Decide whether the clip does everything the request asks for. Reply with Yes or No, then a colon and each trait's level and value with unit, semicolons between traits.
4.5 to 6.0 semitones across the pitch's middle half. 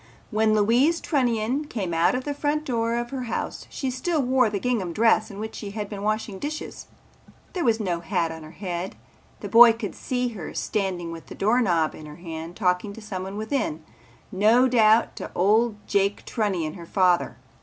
Yes: average, 4.8 semitones